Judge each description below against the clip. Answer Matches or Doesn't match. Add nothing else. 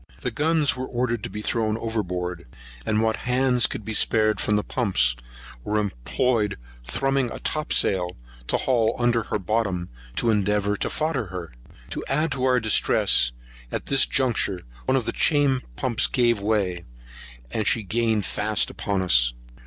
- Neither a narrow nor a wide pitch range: Matches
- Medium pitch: Doesn't match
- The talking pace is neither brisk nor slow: Matches